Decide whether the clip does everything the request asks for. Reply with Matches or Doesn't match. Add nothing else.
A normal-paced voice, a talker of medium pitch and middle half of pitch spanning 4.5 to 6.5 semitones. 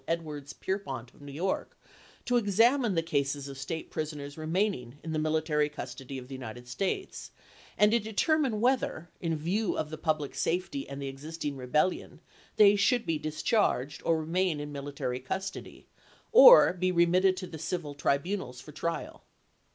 Matches